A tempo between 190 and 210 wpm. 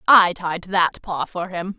Yes: average, 200 wpm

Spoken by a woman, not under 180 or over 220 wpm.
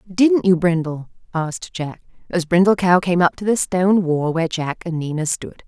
Yes: female; average, 200 wpm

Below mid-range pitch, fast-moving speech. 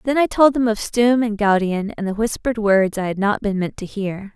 No: high, 215 Hz; fast, 260 wpm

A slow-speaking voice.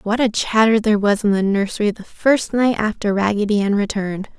No: fast, 205 wpm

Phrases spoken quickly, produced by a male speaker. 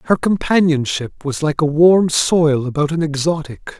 No: average, 160 wpm; male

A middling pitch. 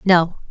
Yes: medium, 175 Hz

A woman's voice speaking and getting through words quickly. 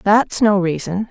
No: female; average, 160 wpm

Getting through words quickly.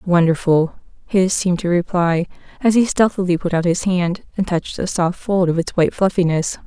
No: average, 190 wpm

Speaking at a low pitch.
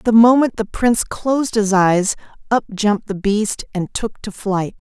No: high, 210 Hz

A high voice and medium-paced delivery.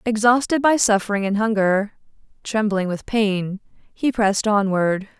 No: high, 210 Hz; slow, 125 wpm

